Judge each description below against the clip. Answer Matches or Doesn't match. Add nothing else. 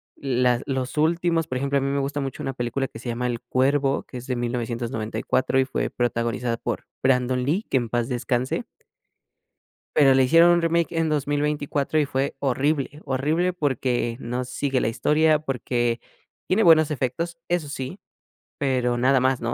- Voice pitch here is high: Doesn't match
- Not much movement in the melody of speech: Doesn't match